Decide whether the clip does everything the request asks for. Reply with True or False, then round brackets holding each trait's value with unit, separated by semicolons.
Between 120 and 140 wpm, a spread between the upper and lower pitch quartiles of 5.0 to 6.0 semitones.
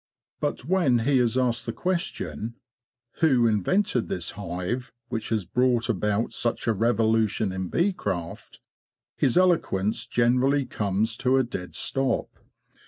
False (135 wpm; 3.8 semitones)